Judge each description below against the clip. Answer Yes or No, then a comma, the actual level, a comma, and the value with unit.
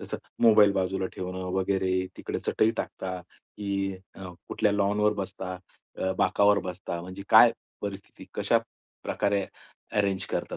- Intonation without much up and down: Yes, narrow, 1.6 semitones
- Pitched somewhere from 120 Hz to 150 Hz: No, very low, 95 Hz